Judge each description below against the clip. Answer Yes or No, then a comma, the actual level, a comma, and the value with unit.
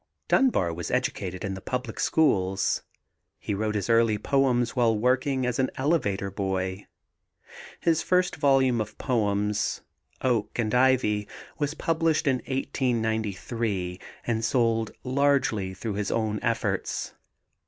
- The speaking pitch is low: Yes, low, 115 Hz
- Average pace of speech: No, slow, 125 wpm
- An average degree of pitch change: Yes, average, 4.3 semitones